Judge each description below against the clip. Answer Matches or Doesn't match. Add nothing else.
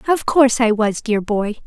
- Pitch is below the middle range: Doesn't match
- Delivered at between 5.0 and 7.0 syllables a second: Doesn't match